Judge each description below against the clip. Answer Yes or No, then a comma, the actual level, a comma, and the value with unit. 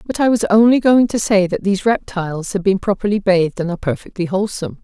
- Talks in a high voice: Yes, high, 200 Hz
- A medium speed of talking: No, fast, 225 wpm